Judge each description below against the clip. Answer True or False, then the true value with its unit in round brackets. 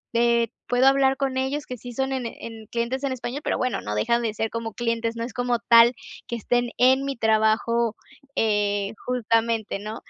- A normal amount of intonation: False (2.1 semitones)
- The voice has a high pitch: True (235 Hz)